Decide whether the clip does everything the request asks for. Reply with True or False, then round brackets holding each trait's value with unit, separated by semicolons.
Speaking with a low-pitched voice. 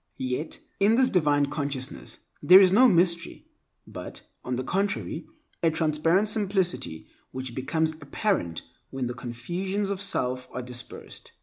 False (160 Hz)